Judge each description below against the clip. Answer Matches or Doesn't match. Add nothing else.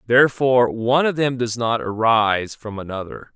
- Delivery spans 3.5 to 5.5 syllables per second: Matches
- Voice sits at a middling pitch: Doesn't match